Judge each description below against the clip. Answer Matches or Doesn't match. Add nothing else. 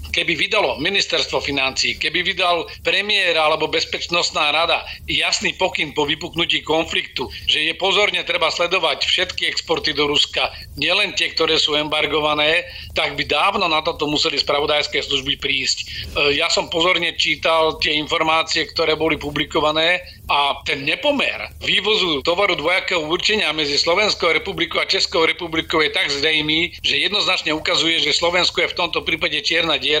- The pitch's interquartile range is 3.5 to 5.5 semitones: Doesn't match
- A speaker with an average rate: Matches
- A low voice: Doesn't match